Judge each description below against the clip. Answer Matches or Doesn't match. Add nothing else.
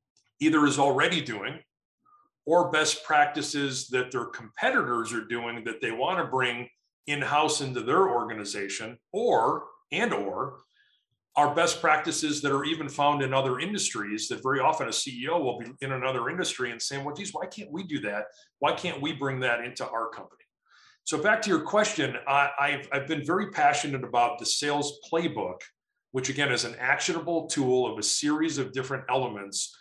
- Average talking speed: Matches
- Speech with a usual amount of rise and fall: Matches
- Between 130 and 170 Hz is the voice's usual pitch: Matches